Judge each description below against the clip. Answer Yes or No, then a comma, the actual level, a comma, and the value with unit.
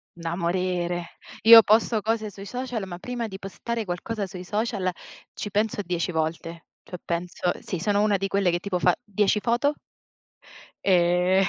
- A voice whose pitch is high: Yes, high, 195 Hz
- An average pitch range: Yes, average, 3.4 semitones